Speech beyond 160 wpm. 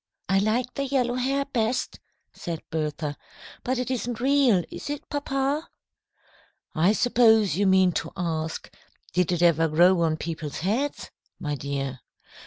No: average, 145 wpm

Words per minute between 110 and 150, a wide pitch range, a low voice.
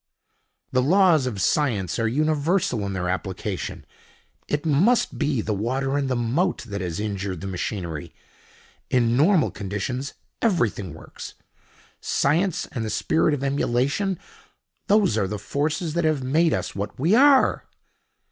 Yes: average, 140 wpm; wide, 7.4 semitones; low, 130 Hz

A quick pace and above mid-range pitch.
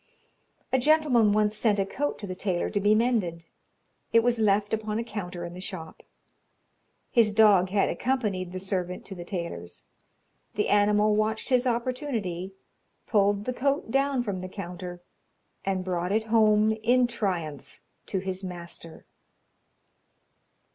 No: average, 150 wpm; high, 205 Hz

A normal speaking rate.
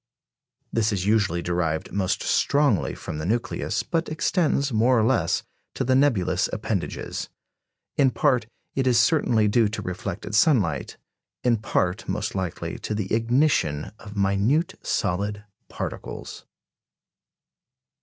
No: slow, 125 wpm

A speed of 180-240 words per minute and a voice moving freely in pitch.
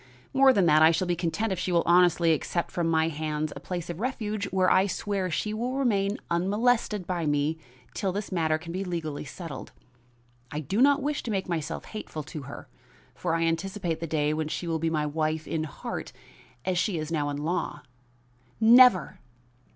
No: average, 195 wpm; average, 4.0 semitones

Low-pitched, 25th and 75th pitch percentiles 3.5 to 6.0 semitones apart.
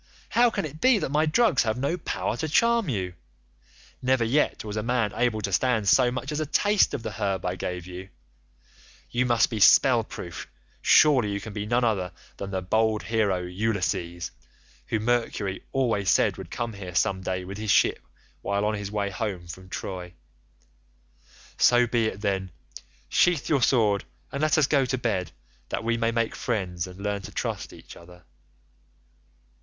Yes: low, 110 Hz; average, 4.7 semitones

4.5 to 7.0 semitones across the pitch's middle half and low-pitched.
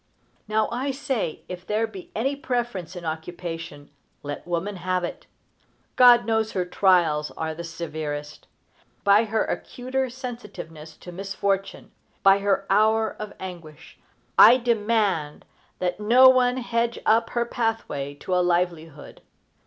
No: wide, 5.4 semitones; high, 195 Hz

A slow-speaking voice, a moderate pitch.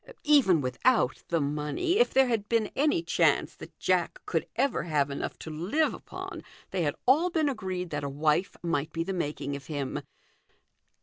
No: average, 180 wpm; medium, 175 Hz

